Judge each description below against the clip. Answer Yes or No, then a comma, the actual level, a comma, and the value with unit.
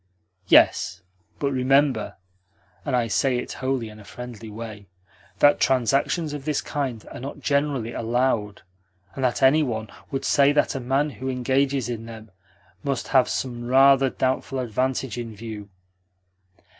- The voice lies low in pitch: Yes, low, 130 Hz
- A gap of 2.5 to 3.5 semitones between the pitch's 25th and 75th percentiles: Yes, average, 3.0 semitones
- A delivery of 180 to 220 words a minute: No, average, 150 wpm